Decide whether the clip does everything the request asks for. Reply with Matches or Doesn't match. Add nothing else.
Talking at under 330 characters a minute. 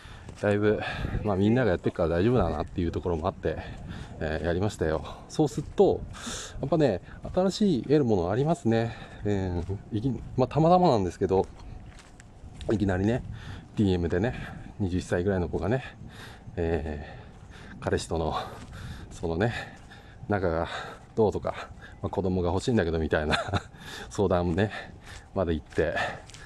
Matches